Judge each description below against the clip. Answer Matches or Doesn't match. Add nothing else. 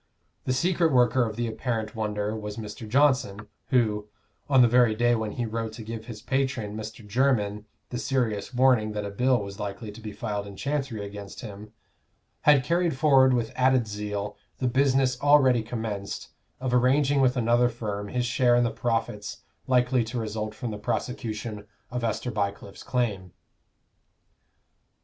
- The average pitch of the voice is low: Matches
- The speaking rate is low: Doesn't match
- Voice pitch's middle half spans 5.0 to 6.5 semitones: Doesn't match